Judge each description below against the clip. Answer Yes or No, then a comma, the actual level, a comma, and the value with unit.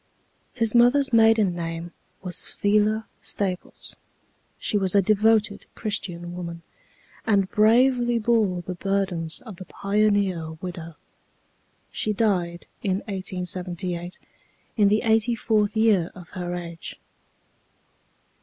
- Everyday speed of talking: No, slow, 110 wpm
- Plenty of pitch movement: No, average, 3.6 semitones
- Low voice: No, high, 200 Hz